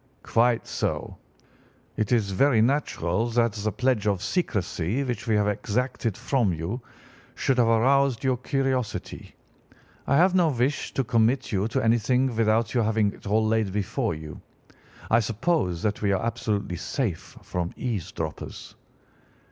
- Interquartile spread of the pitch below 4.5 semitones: Yes, average, 3.6 semitones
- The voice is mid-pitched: No, low, 115 Hz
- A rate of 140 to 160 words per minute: Yes, average, 150 wpm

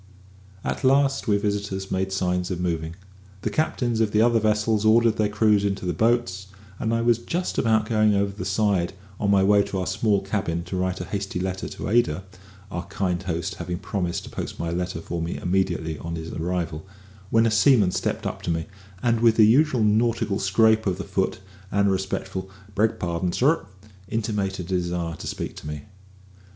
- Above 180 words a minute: Yes, average, 195 wpm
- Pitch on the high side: No, low, 100 Hz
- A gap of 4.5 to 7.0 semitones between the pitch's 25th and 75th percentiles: No, average, 3.6 semitones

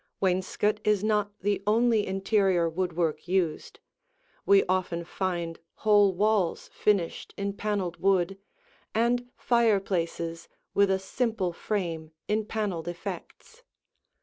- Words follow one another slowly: Yes, slow, 110 wpm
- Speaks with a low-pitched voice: No, high, 195 Hz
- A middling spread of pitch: Yes, average, 3.2 semitones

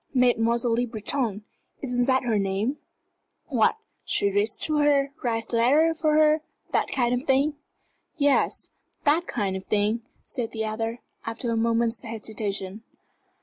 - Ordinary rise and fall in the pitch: Yes, average, 3.8 semitones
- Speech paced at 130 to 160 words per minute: Yes, average, 145 wpm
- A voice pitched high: Yes, high, 235 Hz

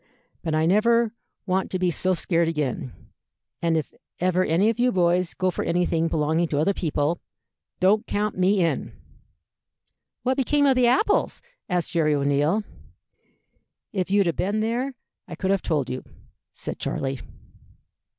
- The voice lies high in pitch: No, medium, 180 Hz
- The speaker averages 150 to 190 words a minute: Yes, average, 160 wpm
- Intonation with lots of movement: No, average, 4.5 semitones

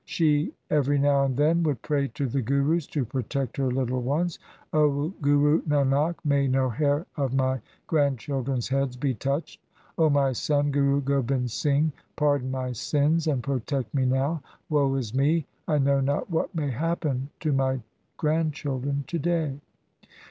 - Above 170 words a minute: No, average, 160 wpm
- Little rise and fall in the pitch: Yes, narrow, 2.1 semitones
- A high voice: No, medium, 140 Hz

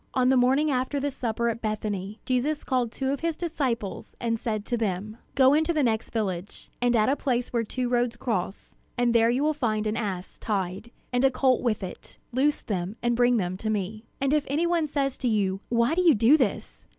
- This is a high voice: Yes, high, 240 Hz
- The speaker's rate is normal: No, fast, 225 wpm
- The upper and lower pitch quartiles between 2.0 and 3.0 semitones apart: No, average, 3.8 semitones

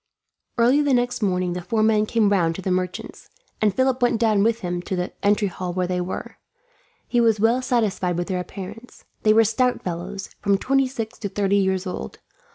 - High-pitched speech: Yes, high, 205 Hz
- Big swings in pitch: No, average, 4.1 semitones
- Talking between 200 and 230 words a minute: Yes, fast, 205 wpm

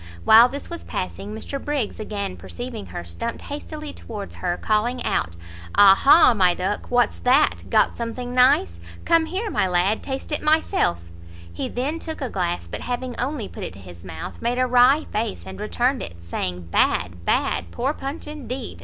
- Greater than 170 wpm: Yes, average, 180 wpm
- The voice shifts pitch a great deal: Yes, wide, 6.8 semitones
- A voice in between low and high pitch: No, high, 240 Hz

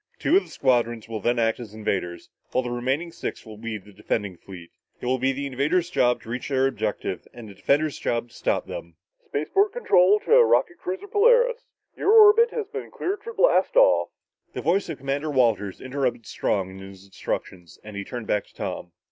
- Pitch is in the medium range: No, low, 130 Hz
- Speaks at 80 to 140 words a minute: No, fast, 205 wpm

